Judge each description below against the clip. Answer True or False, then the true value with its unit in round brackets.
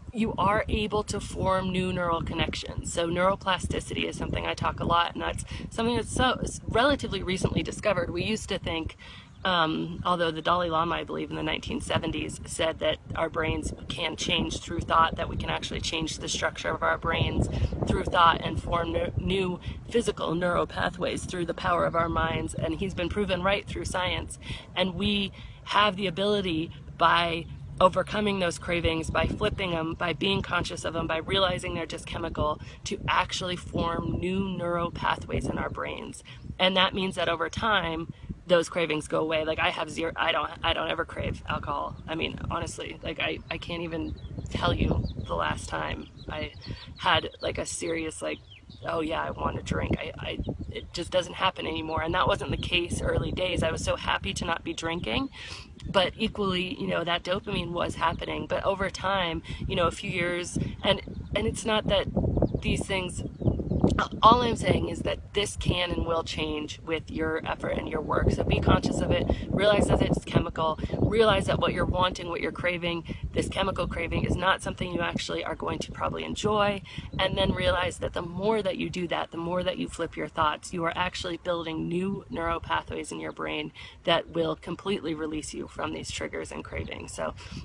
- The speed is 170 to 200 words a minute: True (195 wpm)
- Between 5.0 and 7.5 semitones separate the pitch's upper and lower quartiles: False (2.7 semitones)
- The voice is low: False (170 Hz)